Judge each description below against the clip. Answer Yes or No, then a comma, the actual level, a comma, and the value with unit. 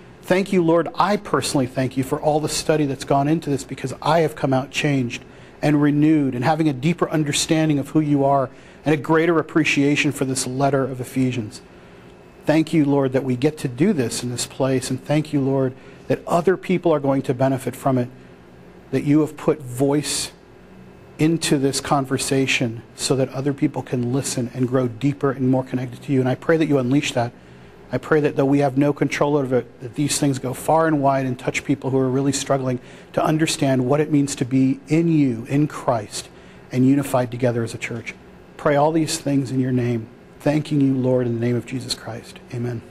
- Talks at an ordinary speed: No, fast, 215 wpm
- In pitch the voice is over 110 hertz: Yes, medium, 140 Hz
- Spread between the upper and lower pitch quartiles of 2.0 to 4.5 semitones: Yes, average, 2.7 semitones